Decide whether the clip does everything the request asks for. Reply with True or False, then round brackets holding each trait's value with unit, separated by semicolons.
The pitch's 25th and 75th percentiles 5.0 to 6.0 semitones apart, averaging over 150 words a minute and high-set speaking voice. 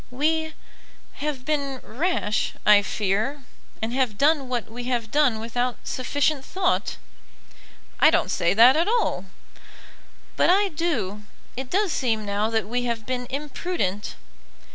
False (5.5 semitones; 140 wpm; 255 Hz)